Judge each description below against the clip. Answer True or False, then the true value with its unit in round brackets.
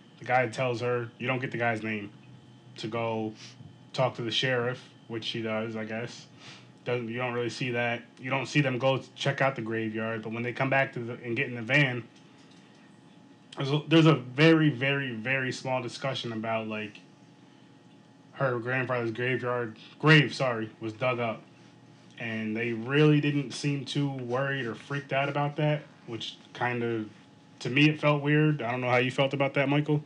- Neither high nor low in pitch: False (125 Hz)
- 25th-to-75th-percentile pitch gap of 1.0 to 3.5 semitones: True (3.2 semitones)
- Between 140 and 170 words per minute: False (190 wpm)